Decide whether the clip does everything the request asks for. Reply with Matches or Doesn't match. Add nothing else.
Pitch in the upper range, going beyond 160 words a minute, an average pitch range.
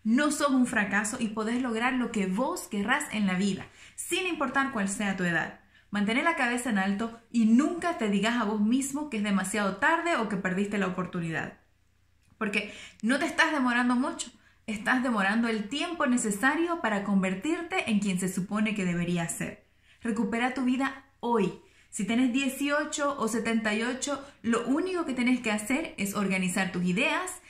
Matches